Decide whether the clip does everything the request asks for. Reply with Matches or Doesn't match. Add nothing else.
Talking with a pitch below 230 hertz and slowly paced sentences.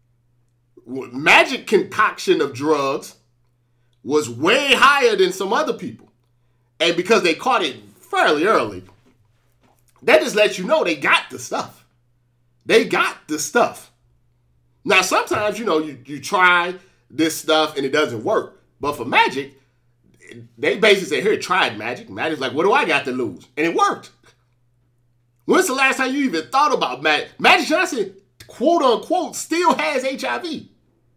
Doesn't match